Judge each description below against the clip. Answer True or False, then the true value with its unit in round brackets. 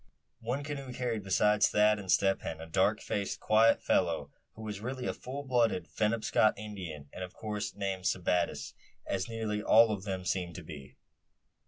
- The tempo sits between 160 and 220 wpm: True (175 wpm)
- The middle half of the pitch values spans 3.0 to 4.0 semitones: True (3.5 semitones)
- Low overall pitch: True (105 Hz)